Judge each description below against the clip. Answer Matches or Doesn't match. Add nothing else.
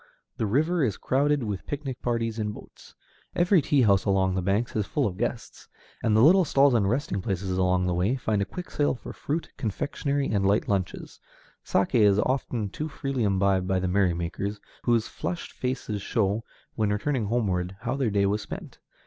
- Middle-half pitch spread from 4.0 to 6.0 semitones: Matches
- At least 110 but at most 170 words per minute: Doesn't match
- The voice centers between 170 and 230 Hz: Doesn't match